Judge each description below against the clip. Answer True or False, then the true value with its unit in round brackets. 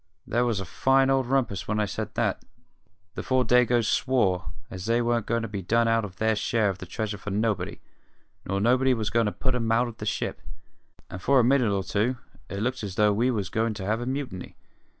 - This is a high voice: False (115 Hz)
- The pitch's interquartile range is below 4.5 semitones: True (3.4 semitones)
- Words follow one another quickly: True (230 wpm)